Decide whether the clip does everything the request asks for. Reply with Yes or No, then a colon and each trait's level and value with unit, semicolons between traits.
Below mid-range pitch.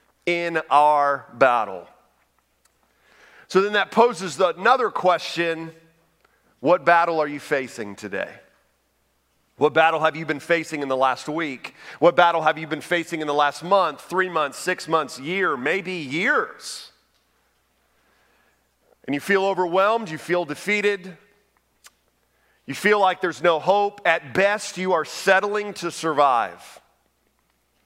No: medium, 165 Hz